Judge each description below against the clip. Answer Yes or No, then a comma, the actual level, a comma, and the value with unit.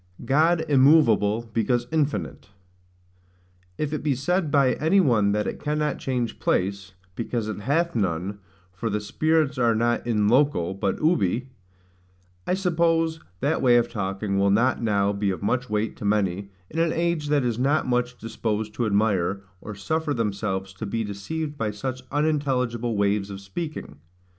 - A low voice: Yes, low, 120 Hz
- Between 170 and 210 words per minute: No, average, 160 wpm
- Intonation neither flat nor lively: No, wide, 6.3 semitones